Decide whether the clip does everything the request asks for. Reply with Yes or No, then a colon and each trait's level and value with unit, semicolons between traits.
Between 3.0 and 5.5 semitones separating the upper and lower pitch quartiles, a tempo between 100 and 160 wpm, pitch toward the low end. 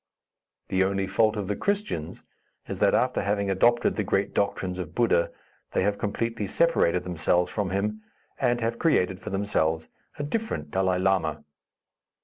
Yes: average, 3.6 semitones; average, 155 wpm; low, 100 Hz